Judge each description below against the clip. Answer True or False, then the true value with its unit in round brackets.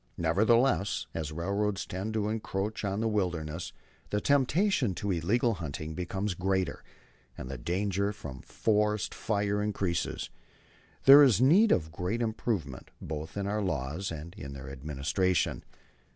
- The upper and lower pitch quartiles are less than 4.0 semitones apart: False (4.7 semitones)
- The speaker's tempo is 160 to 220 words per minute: False (135 wpm)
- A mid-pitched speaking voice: False (95 Hz)